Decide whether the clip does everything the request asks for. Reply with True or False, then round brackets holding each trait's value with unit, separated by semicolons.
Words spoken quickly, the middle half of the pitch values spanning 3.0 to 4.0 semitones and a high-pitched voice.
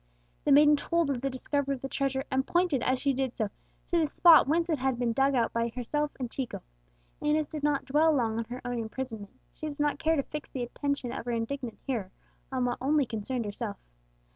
True (225 wpm; 3.5 semitones; 270 Hz)